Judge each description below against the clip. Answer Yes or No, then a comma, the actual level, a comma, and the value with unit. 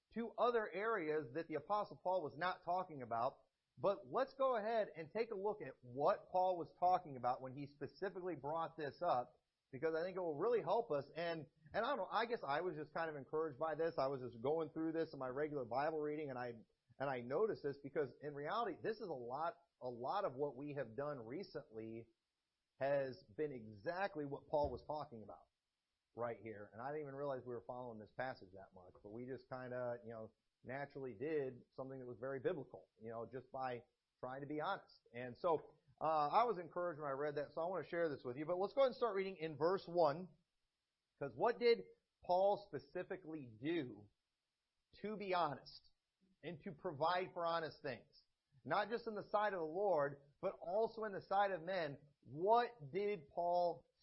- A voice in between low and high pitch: Yes, medium, 155 Hz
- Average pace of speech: No, fast, 210 wpm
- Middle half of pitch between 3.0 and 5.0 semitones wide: No, wide, 5.6 semitones